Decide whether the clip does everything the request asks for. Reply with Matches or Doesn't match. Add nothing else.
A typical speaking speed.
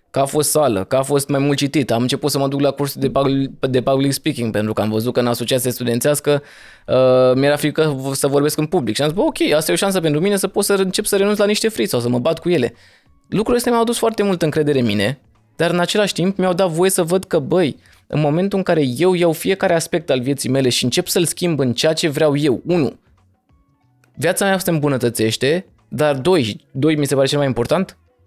Doesn't match